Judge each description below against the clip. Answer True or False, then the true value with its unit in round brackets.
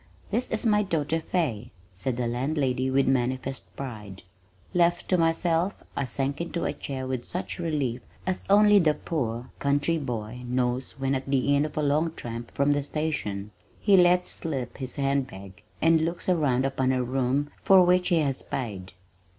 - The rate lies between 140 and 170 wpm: False (180 wpm)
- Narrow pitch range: False (4.7 semitones)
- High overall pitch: False (140 Hz)